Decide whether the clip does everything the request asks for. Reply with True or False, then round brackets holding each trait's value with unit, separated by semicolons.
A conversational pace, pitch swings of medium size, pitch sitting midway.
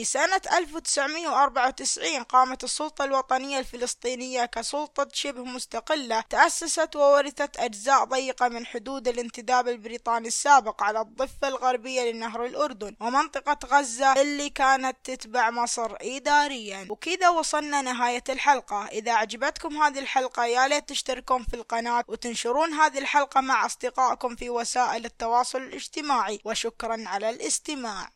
False (120 wpm; 3.1 semitones; 255 Hz)